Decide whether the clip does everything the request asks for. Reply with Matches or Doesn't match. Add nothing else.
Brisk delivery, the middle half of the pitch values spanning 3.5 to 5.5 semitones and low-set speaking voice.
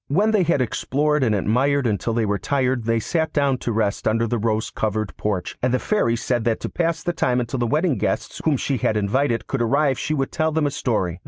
Matches